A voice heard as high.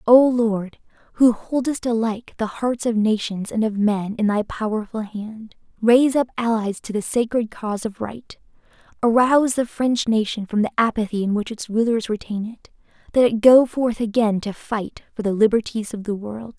Yes: high, 225 Hz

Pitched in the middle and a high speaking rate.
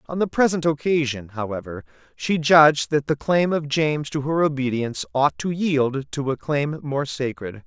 No: medium, 145 Hz; average, 180 wpm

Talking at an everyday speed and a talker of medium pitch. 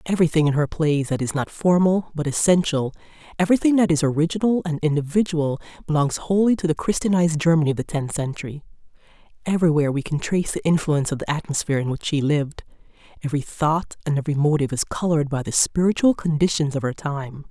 Yes: average, 180 wpm; medium, 155 Hz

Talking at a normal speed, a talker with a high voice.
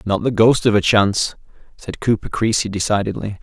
No: average, 175 wpm; low, 105 Hz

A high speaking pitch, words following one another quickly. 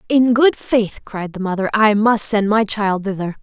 Yes: high, 210 Hz; fast, 210 wpm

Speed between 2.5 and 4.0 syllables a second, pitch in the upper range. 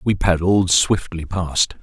No: 3.5 syllables/s; very low, 90 Hz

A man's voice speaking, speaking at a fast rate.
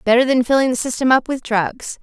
No: female; fast, 235 wpm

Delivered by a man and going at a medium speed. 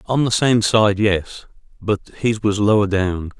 Yes: male; average, 175 wpm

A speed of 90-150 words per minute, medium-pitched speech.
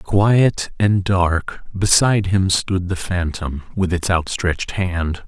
No: slow, 135 wpm; very low, 95 Hz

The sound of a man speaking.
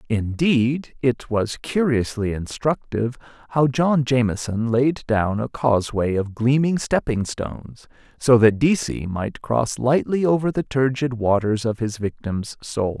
Yes: male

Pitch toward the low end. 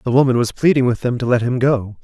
Yes: low, 125 Hz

